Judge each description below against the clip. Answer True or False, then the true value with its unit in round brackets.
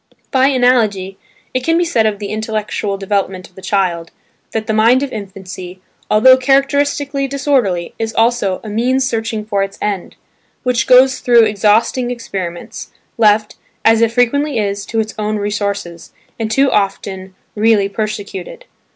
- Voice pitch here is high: True (220 Hz)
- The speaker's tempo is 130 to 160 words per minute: True (150 wpm)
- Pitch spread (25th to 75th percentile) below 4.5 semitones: True (4.0 semitones)